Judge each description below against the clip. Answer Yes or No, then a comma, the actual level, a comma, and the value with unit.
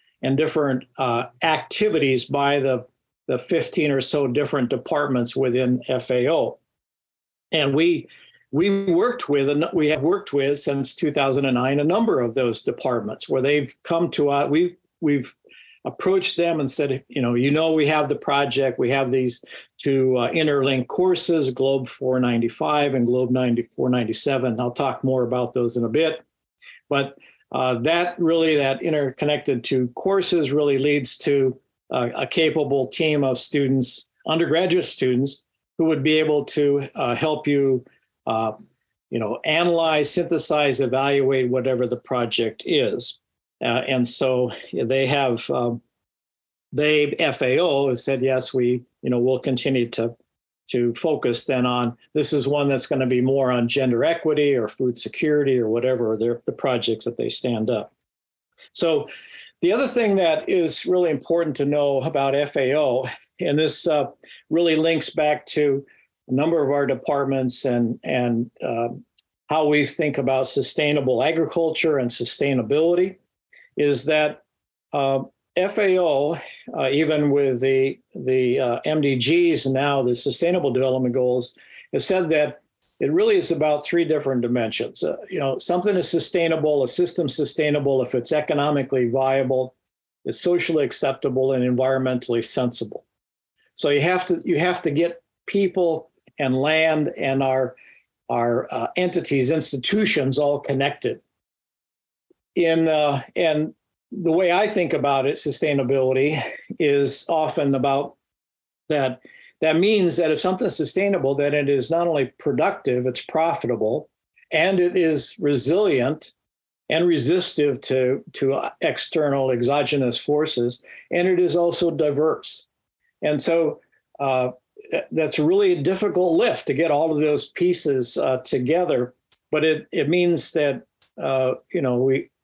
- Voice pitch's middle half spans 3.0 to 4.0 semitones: Yes, average, 3.7 semitones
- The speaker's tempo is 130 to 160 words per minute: Yes, average, 145 wpm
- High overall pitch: No, medium, 140 Hz